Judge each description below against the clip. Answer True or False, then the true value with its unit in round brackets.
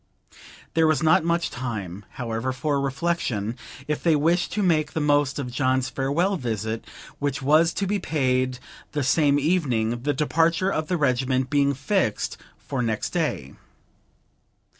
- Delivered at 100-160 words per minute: True (150 wpm)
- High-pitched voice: False (140 Hz)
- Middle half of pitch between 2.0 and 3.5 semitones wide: False (4.2 semitones)